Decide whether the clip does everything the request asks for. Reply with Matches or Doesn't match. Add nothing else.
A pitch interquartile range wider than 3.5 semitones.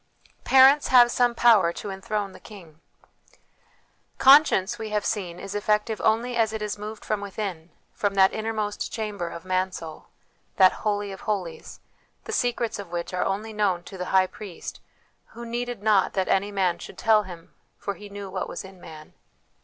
Doesn't match